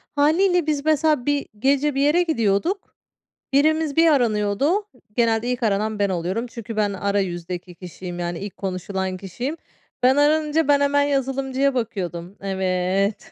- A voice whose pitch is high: Yes, high, 235 Hz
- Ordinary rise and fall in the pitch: No, wide, 6.9 semitones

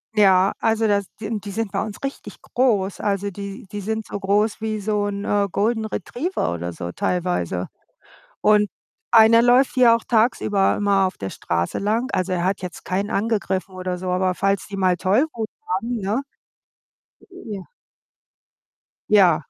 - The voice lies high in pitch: Yes, high, 205 Hz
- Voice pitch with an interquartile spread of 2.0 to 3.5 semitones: Yes, average, 2.9 semitones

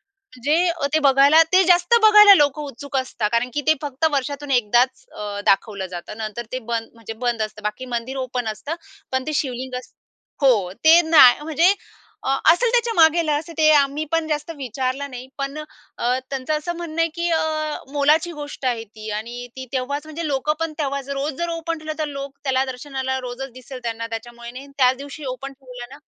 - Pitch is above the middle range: Yes, very high, 275 Hz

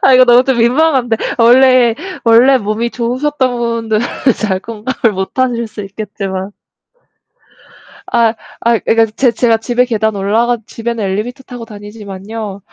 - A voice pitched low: No, high, 230 Hz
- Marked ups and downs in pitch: No, narrow, 2.6 semitones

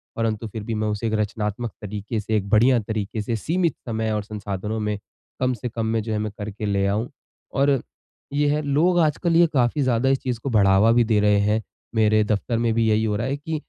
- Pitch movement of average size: Yes, average, 3.0 semitones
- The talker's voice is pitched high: No, low, 110 Hz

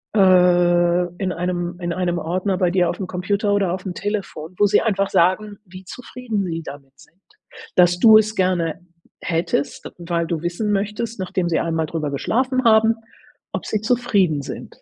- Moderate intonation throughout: Yes, average, 3.2 semitones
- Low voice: No, medium, 185 Hz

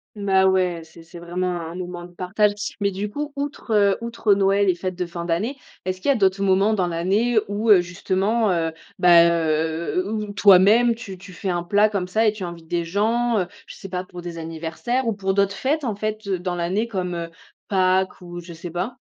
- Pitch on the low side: No, high, 190 Hz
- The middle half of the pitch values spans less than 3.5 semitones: Yes, average, 3.1 semitones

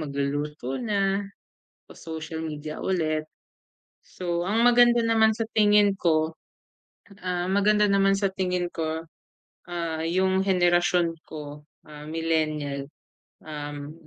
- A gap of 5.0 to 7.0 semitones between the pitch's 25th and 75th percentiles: No, average, 4.1 semitones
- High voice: No, medium, 170 Hz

